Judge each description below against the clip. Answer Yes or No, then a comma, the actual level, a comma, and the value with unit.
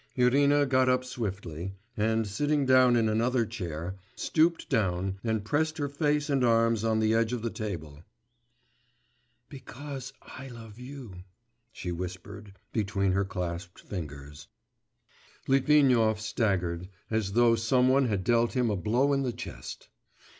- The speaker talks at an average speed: Yes, average, 145 wpm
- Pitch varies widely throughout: No, average, 4.9 semitones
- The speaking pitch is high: No, low, 115 Hz